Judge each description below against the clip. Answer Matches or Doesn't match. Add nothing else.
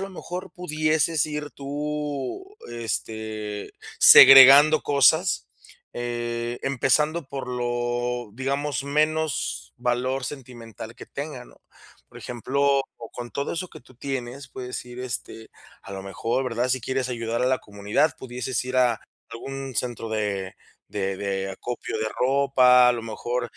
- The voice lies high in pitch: Doesn't match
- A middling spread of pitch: Matches